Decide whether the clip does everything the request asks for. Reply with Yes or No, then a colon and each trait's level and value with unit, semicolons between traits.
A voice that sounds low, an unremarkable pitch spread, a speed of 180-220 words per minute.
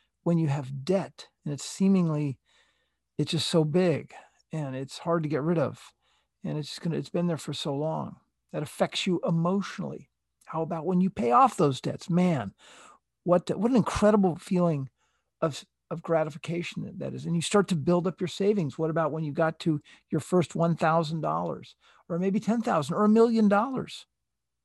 No: medium, 170 Hz; average, 3.1 semitones; average, 190 wpm